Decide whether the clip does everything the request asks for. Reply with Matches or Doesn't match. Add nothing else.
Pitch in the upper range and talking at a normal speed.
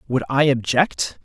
Doesn't match